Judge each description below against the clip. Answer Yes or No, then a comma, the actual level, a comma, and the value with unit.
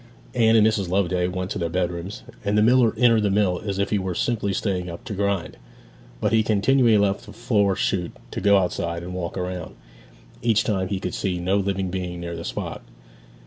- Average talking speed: No, fast, 210 wpm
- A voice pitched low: Yes, very low, 95 Hz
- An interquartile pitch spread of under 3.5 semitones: Yes, average, 2.8 semitones